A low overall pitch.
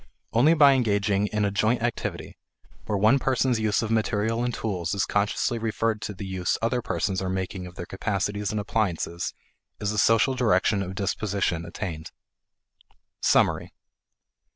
Yes: low, 105 Hz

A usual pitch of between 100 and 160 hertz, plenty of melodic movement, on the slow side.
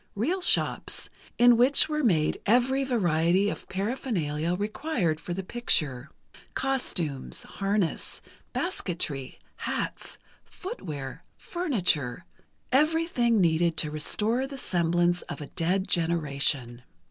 No: medium, 185 Hz; wide, 7.7 semitones; slow, 100 wpm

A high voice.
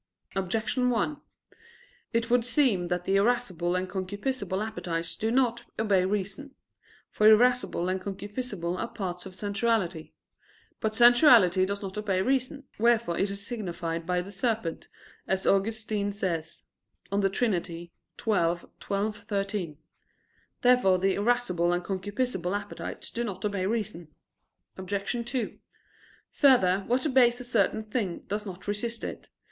Yes: high, 205 Hz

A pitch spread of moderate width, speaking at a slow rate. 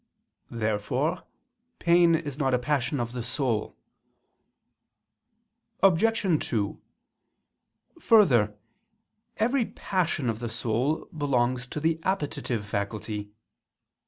No: wide, 6.1 semitones; slow, 95 wpm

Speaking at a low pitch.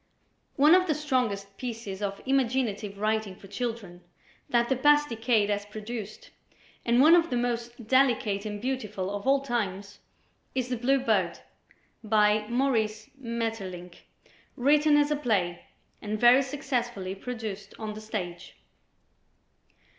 No: high, 225 Hz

